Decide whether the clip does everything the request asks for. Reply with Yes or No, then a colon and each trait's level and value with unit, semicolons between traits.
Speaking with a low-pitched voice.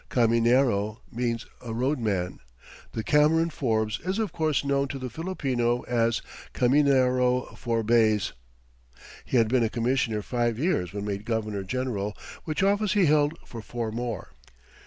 Yes: low, 120 Hz